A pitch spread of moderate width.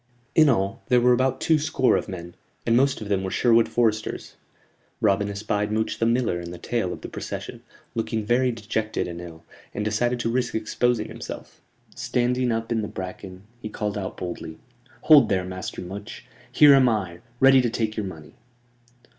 Yes: average, 4.0 semitones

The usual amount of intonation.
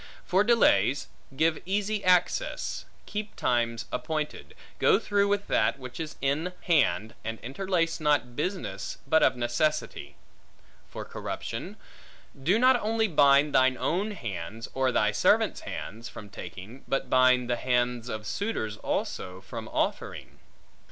No: wide, 7.4 semitones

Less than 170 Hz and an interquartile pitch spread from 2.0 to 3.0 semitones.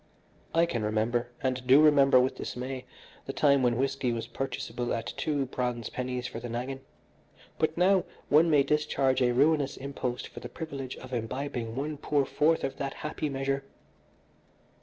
Yes: low, 135 Hz; narrow, 2.6 semitones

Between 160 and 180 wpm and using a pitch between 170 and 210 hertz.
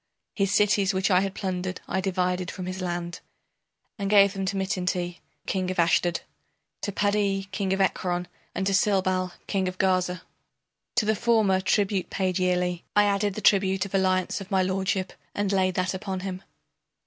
Yes: average, 175 wpm; high, 190 Hz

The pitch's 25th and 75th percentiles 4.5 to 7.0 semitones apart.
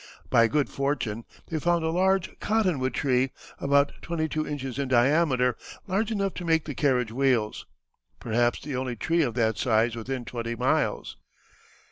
Yes: average, 5.0 semitones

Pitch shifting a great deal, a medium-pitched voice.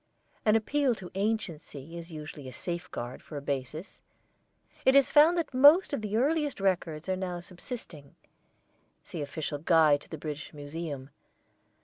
Yes: wide, 7.0 semitones; medium, 170 Hz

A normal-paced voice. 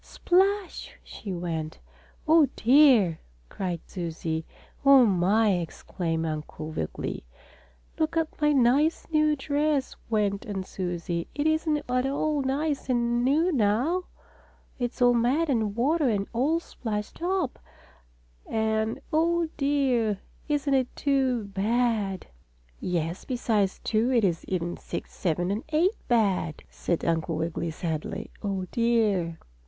No: slow, 125 wpm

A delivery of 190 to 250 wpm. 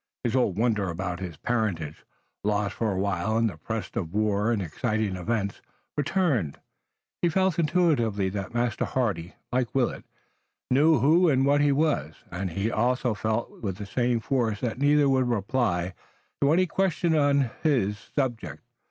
No: average, 170 wpm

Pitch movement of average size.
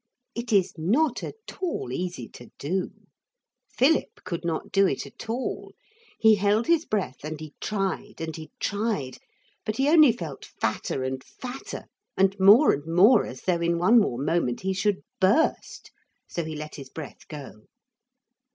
No: wide, 6.2 semitones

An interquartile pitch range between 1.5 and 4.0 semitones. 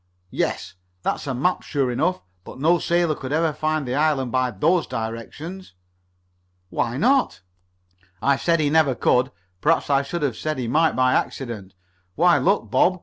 No: average, 4.6 semitones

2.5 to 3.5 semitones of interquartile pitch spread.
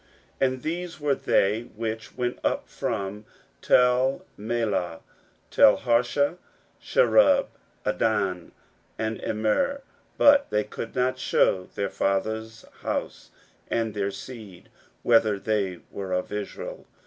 No: average, 4.2 semitones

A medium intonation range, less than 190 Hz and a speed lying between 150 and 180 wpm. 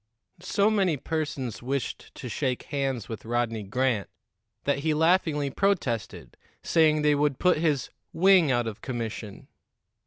No: average, 5.0 semitones; medium, 140 Hz; slow, 135 wpm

